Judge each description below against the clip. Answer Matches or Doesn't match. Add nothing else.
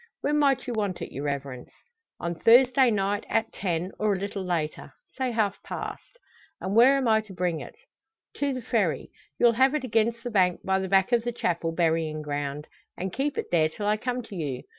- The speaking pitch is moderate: Doesn't match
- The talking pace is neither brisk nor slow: Doesn't match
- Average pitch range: Doesn't match